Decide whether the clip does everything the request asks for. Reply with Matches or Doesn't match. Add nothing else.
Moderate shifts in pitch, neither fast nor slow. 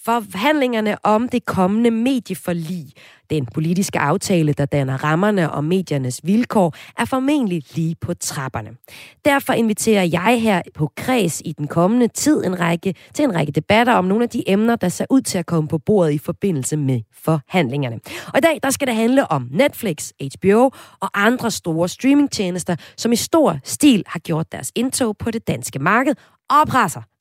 Doesn't match